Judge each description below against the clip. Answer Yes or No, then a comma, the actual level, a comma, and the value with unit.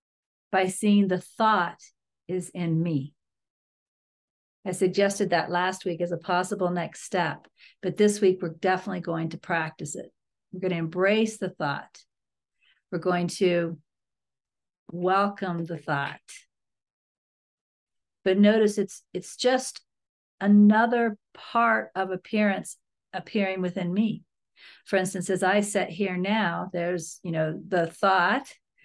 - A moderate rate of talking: No, slow, 130 wpm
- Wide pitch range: No, average, 2.7 semitones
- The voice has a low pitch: No, medium, 185 Hz